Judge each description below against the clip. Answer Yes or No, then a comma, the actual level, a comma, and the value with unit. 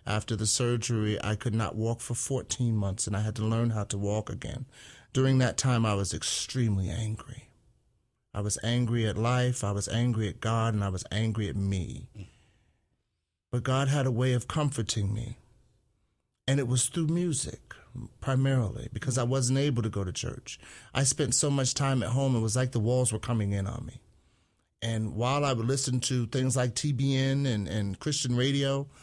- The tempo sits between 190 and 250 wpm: Yes, average, 195 wpm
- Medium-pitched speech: No, low, 120 Hz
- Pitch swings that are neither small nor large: Yes, average, 3.3 semitones